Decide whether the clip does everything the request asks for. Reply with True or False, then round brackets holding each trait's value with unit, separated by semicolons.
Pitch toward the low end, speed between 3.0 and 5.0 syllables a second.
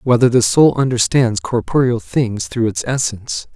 True (125 Hz; 4.6 syllables/s)